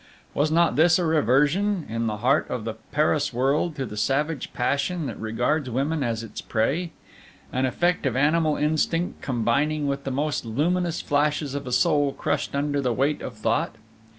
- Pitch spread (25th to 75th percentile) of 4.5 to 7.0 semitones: No, average, 3.9 semitones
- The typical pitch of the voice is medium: Yes, medium, 145 Hz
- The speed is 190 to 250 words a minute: No, average, 180 wpm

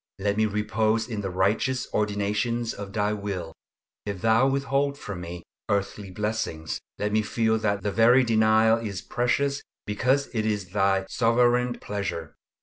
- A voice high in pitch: No, low, 105 Hz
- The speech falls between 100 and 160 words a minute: Yes, average, 150 wpm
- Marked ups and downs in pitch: No, narrow, 2.6 semitones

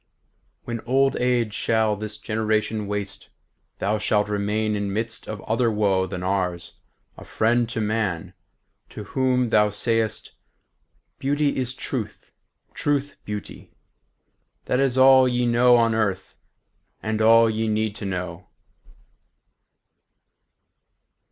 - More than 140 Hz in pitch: No, low, 110 Hz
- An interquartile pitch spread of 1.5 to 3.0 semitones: Yes, average, 2.7 semitones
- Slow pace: Yes, slow, 120 wpm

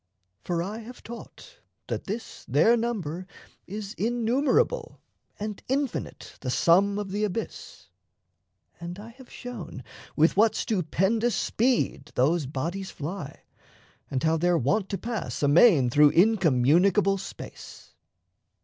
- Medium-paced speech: No, slow, 120 wpm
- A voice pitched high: Yes, high, 195 Hz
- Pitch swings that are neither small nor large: No, wide, 5.8 semitones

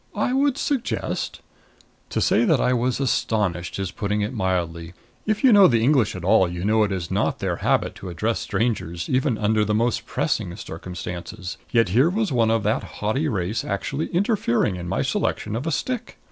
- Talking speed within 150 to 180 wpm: No, average, 195 wpm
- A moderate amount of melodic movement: No, wide, 6.5 semitones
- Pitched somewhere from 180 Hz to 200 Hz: No, low, 110 Hz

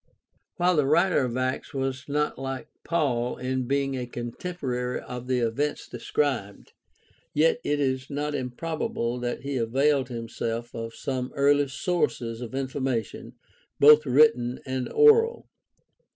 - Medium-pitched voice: No, low, 130 Hz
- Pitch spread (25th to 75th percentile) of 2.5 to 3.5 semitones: Yes, average, 3.0 semitones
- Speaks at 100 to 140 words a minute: Yes, slow, 135 wpm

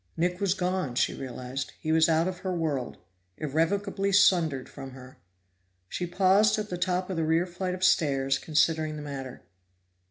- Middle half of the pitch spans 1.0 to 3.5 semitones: No, average, 4.6 semitones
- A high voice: No, medium, 165 Hz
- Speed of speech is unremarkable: Yes, average, 170 wpm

